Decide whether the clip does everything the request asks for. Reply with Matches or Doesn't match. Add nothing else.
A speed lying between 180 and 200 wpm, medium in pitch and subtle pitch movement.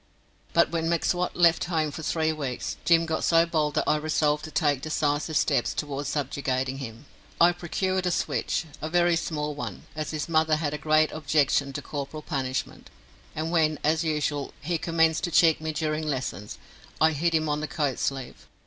Matches